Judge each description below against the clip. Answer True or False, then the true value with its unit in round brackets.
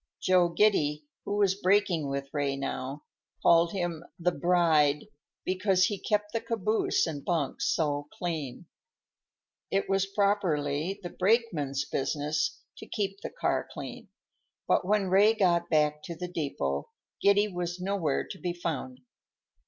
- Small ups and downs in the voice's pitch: False (4.8 semitones)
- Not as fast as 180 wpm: True (140 wpm)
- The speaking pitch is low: False (175 Hz)